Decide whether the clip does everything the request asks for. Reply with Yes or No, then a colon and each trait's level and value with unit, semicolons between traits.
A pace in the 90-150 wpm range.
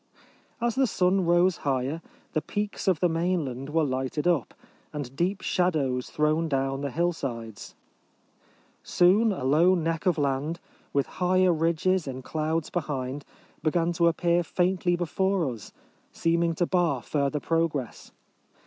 Yes: average, 140 wpm